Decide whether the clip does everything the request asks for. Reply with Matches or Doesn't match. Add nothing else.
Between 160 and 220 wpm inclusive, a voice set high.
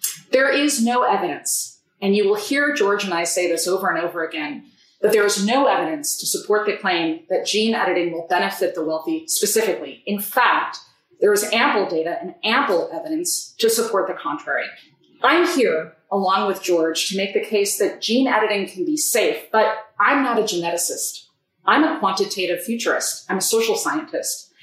Matches